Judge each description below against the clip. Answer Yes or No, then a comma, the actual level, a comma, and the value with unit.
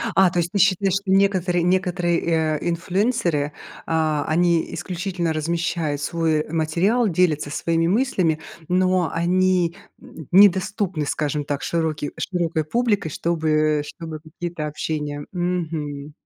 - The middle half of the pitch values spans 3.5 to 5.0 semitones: No, average, 2.8 semitones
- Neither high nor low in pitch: Yes, medium, 170 Hz